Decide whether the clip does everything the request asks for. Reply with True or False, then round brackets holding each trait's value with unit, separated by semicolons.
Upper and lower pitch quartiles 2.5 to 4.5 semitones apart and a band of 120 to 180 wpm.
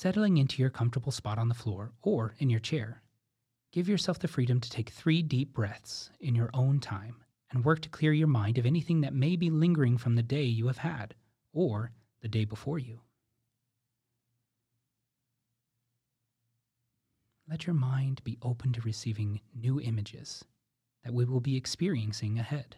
True (2.9 semitones; 165 wpm)